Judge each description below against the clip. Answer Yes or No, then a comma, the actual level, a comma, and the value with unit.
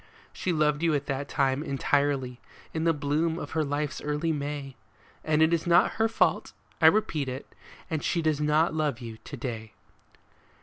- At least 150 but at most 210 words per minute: Yes, average, 180 wpm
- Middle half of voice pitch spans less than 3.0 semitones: Yes, narrow, 2.4 semitones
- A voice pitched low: No, medium, 150 Hz